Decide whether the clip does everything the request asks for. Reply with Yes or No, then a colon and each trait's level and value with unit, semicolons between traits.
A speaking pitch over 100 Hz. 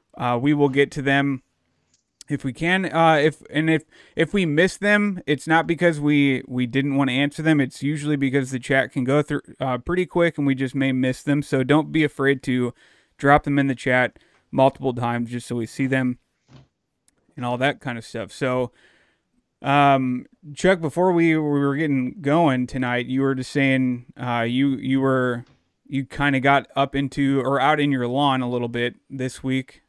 Yes: low, 135 Hz